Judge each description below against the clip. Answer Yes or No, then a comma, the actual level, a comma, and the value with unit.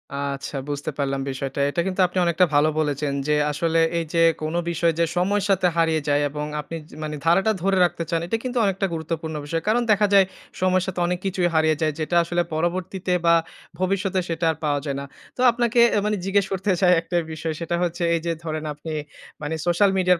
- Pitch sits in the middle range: Yes, medium, 170 Hz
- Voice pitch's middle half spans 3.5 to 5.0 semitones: No, average, 3.1 semitones